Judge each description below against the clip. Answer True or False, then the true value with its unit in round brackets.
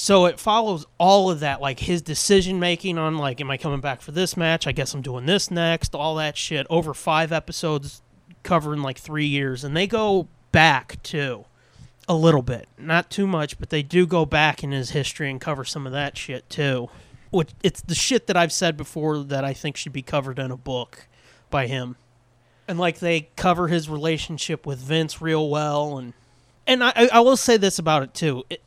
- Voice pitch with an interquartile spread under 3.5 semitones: False (4.0 semitones)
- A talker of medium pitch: True (155 Hz)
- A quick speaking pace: True (210 wpm)